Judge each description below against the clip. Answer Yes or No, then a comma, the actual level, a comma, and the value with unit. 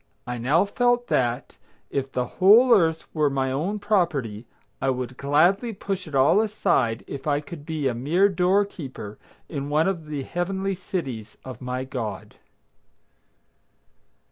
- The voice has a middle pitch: Yes, medium, 150 Hz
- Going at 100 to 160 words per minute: Yes, average, 150 wpm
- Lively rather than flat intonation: Yes, wide, 6.7 semitones